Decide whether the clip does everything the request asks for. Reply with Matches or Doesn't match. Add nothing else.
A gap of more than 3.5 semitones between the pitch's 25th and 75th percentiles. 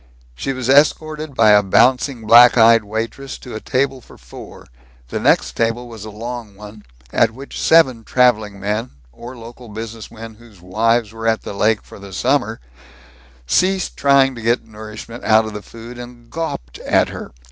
Doesn't match